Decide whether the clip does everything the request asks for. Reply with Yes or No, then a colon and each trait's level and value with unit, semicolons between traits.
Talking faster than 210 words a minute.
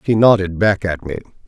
No: fast, 205 wpm